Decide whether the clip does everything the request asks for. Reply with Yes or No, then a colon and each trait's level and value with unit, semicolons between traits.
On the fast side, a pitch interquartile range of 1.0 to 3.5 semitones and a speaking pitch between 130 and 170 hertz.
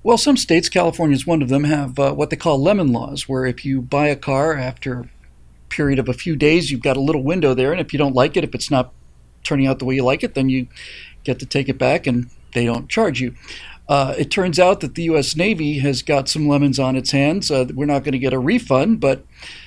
Yes: fast, 260 wpm; average, 2.7 semitones; medium, 140 Hz